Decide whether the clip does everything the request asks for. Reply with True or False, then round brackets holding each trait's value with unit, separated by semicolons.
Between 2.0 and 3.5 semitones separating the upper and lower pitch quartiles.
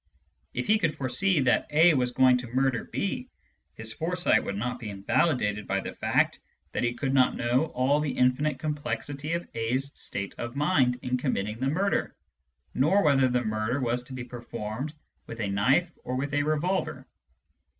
False (4.0 semitones)